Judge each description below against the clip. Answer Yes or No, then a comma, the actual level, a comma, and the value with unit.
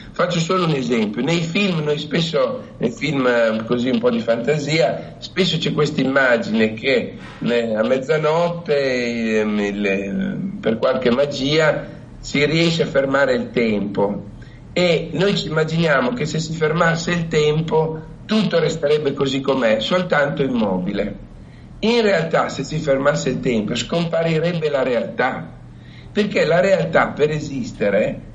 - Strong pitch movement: No, average, 4.7 semitones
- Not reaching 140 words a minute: Yes, average, 130 wpm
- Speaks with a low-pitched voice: No, medium, 150 Hz